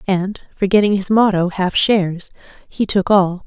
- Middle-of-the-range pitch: No, high, 195 Hz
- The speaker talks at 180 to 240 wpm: No, average, 155 wpm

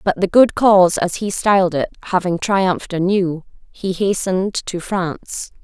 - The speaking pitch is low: No, medium, 185 Hz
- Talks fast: No, average, 160 wpm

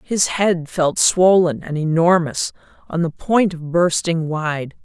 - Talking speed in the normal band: Yes, average, 150 wpm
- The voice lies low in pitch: No, medium, 170 Hz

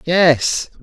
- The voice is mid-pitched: Yes, medium, 160 Hz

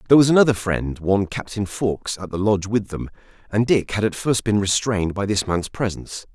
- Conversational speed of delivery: No, fast, 215 wpm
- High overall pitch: No, low, 105 Hz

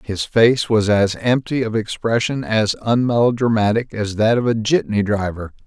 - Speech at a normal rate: Yes, average, 160 wpm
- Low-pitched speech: Yes, low, 110 Hz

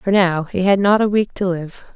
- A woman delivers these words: Yes, female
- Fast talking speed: Yes, fast, 275 wpm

